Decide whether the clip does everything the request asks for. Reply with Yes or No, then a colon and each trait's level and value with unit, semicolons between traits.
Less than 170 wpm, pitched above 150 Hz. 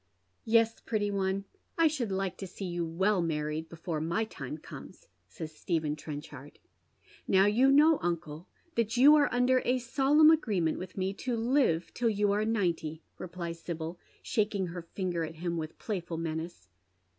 No: average, 175 wpm; high, 190 Hz